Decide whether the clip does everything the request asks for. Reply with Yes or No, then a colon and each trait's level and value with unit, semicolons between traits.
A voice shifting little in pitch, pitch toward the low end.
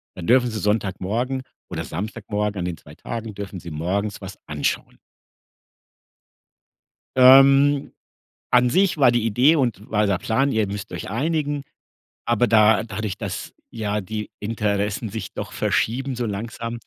No: average, 3.5 semitones; low, 110 Hz